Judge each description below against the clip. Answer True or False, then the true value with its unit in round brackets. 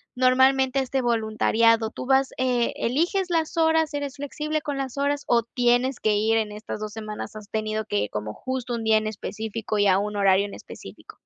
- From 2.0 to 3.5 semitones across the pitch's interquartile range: False (3.9 semitones)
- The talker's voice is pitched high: True (235 Hz)